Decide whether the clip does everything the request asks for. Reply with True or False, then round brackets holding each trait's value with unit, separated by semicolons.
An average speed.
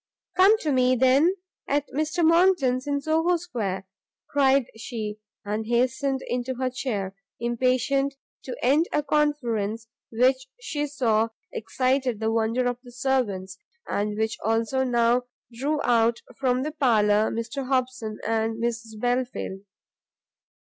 False (130 wpm)